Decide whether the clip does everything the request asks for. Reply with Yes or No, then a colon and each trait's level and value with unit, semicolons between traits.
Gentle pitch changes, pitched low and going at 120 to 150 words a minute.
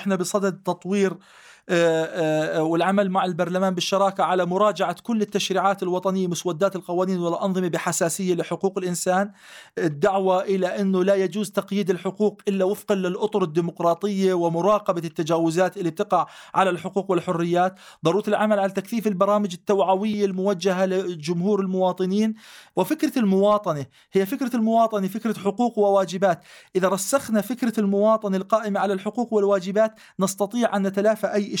No: narrow, 2.1 semitones; high, 195 Hz; average, 125 wpm